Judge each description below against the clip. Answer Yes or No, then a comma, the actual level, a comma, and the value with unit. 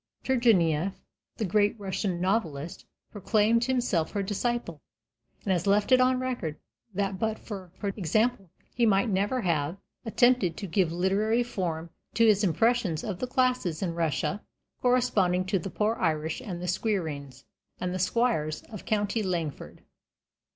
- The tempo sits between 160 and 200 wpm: No, average, 150 wpm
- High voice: Yes, high, 195 Hz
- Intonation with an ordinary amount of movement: Yes, average, 4.7 semitones